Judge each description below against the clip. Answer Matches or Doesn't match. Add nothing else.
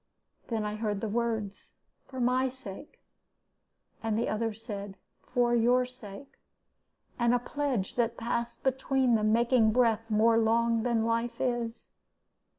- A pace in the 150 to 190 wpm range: Doesn't match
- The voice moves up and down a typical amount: Doesn't match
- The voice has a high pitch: Matches